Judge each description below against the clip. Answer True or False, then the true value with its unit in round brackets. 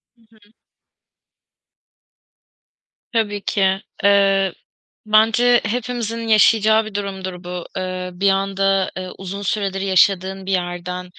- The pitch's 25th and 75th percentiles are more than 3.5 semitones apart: False (2.4 semitones)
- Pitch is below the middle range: False (195 Hz)